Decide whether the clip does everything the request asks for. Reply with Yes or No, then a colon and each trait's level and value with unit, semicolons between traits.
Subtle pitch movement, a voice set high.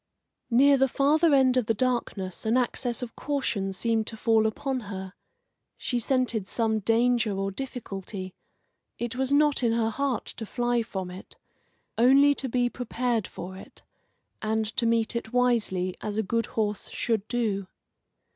No: average, 3.2 semitones; high, 230 Hz